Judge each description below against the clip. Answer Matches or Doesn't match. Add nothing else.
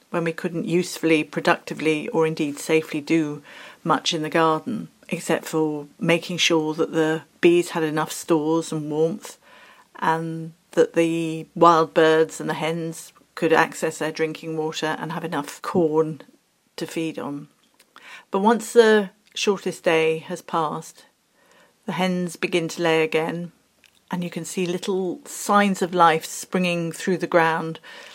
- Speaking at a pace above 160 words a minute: Doesn't match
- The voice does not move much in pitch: Matches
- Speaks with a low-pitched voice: Doesn't match